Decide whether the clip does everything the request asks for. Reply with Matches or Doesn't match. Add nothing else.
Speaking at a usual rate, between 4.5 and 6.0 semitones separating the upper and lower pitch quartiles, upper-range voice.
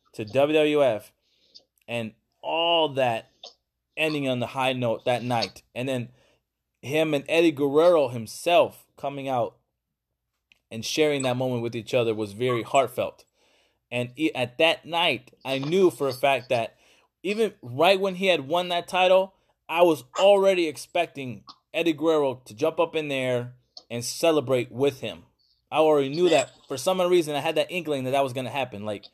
Doesn't match